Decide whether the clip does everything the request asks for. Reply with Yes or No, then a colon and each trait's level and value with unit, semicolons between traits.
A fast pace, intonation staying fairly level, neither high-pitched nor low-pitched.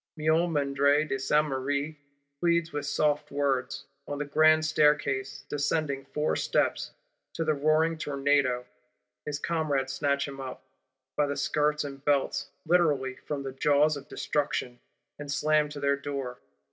No: average, 140 wpm; narrow, 1.7 semitones; medium, 145 Hz